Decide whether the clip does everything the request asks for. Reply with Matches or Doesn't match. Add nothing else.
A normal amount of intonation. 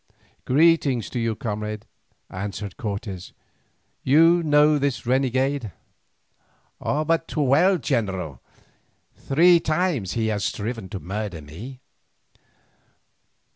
Doesn't match